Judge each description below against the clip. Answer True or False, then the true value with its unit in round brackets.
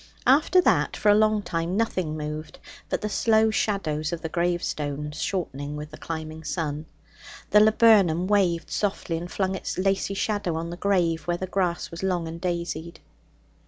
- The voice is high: False (175 Hz)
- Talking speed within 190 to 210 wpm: False (170 wpm)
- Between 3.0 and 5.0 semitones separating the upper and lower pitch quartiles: True (3.9 semitones)